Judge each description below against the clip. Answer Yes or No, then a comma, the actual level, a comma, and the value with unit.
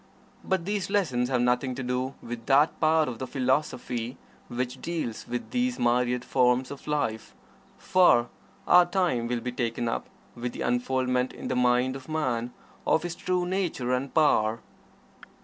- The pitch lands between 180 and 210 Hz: No, low, 125 Hz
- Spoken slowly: No, average, 165 wpm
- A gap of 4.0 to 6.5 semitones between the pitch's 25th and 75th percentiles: Yes, average, 4.3 semitones